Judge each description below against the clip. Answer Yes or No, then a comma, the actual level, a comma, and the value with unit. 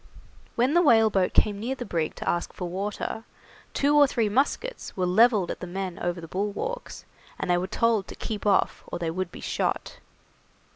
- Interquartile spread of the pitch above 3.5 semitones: Yes, average, 4.7 semitones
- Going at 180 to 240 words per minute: Yes, average, 195 wpm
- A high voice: Yes, high, 205 Hz